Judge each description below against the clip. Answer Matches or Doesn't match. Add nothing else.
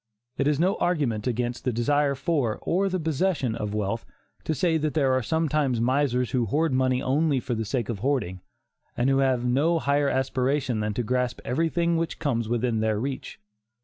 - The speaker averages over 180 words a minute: Matches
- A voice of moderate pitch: Doesn't match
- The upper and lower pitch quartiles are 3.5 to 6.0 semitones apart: Matches